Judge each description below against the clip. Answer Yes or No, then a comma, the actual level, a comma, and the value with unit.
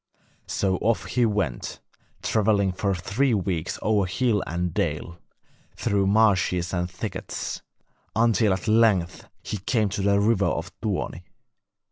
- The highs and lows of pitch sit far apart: No, average, 3.2 semitones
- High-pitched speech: No, low, 100 Hz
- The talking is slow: Yes, slow, 130 wpm